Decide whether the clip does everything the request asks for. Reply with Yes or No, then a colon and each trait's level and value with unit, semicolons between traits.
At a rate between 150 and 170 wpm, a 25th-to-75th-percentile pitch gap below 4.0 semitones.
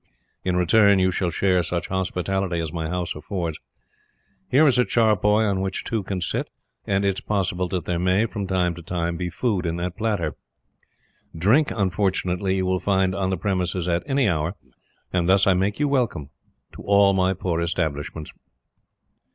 No: average, 180 wpm; narrow, 2.4 semitones